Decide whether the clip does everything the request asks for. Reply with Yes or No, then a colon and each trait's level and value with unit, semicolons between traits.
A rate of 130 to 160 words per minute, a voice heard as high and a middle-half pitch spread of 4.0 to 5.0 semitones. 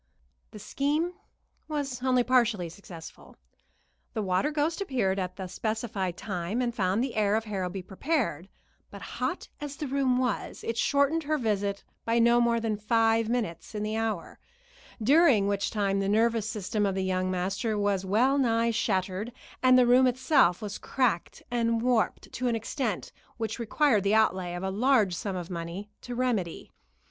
No: average, 170 wpm; high, 220 Hz; average, 4.3 semitones